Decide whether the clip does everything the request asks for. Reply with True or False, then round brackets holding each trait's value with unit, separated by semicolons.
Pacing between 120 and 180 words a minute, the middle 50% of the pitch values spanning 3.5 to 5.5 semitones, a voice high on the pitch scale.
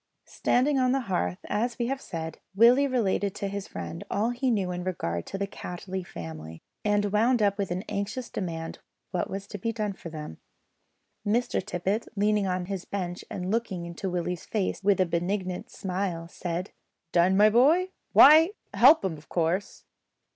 True (175 wpm; 4.1 semitones; 195 Hz)